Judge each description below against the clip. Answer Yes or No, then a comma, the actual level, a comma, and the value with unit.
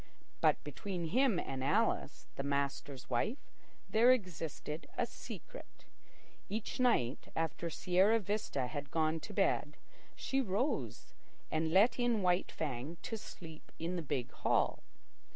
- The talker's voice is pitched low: No, medium, 175 Hz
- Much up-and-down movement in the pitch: Yes, wide, 6.8 semitones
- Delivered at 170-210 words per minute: No, slow, 135 wpm